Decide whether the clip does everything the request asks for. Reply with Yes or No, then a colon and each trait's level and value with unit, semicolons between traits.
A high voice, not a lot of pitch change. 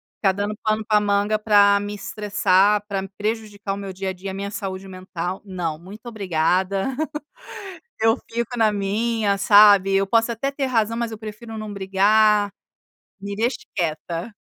Yes: high, 205 Hz; narrow, 2.0 semitones